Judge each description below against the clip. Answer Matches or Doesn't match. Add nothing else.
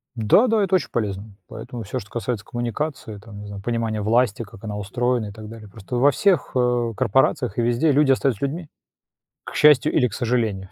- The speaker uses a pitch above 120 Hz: Doesn't match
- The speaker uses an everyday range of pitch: Matches